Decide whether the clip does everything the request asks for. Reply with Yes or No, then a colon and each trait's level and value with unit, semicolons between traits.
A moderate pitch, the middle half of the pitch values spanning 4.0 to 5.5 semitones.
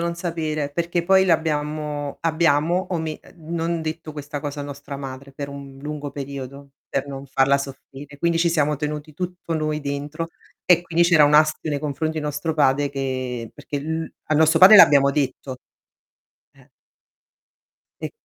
No: medium, 150 Hz; narrow, 2.5 semitones